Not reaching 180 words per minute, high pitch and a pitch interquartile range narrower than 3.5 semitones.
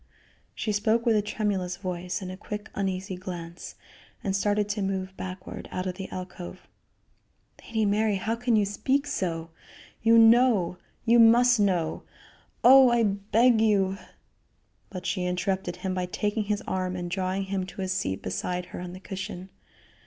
Yes: average, 165 wpm; high, 195 Hz; average, 2.9 semitones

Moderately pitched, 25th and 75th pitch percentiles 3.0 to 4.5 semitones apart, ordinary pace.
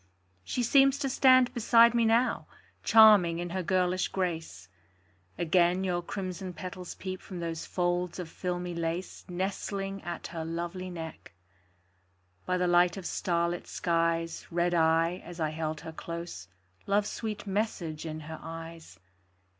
No: medium, 175 Hz; narrow, 2.4 semitones; average, 145 wpm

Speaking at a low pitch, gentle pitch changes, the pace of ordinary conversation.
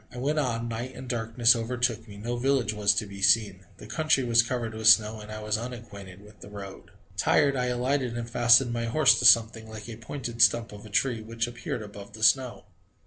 No: low, 115 Hz; narrow, 2.3 semitones; fast, 220 wpm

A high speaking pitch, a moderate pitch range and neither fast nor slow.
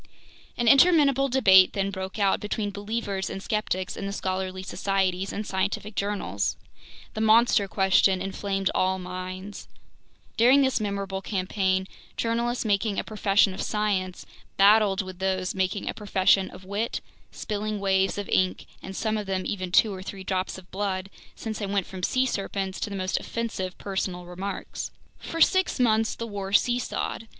No: high, 195 Hz; narrow, 2.2 semitones; average, 160 wpm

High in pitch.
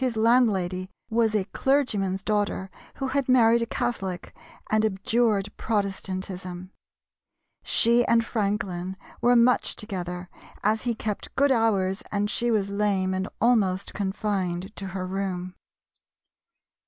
Yes: high, 205 Hz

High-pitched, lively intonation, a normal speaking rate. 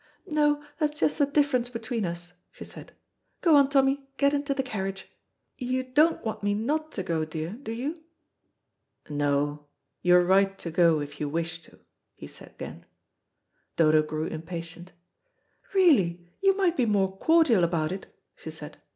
Yes: high, 205 Hz; wide, 8.9 semitones; average, 165 wpm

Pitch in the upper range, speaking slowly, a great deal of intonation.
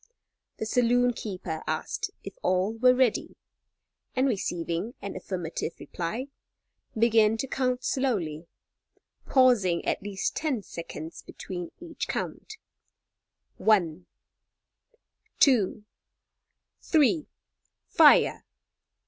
Yes: high, 220 Hz; slow, 90 wpm; wide, 6.1 semitones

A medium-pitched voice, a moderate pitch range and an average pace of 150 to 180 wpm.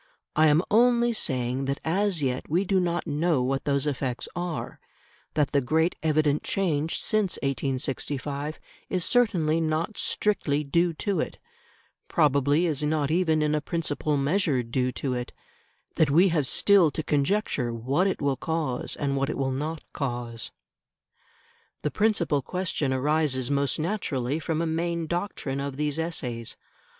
Yes: medium, 150 Hz; average, 3.7 semitones; average, 155 wpm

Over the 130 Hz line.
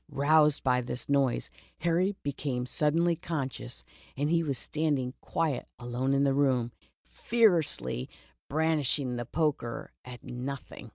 Yes: medium, 140 Hz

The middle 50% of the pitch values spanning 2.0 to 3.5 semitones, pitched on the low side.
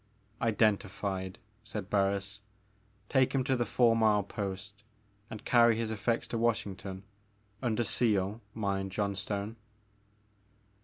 Yes: narrow, 2.5 semitones; low, 105 Hz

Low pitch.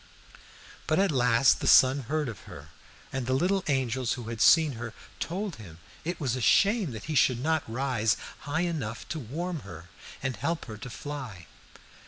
Yes: low, 130 Hz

